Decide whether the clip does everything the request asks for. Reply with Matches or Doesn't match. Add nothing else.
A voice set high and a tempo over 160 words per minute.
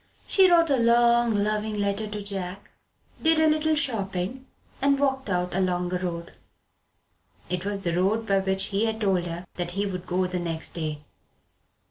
Matches